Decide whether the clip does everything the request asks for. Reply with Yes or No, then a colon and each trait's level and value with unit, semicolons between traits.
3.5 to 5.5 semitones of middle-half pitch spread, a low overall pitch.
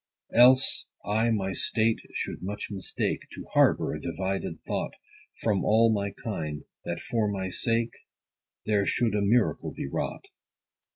No: average, 2.9 semitones; low, 105 Hz